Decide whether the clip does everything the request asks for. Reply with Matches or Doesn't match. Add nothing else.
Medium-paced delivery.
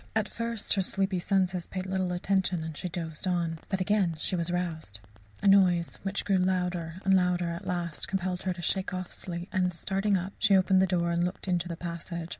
Doesn't match